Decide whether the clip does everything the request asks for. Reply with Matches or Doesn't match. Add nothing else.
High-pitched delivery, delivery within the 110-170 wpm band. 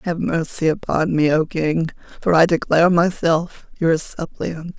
Doesn't match